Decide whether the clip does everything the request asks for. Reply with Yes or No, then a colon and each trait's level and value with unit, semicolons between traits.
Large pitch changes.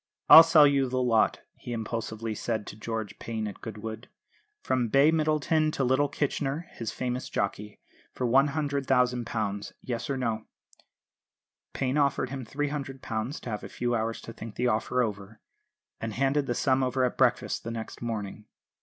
No: average, 3.6 semitones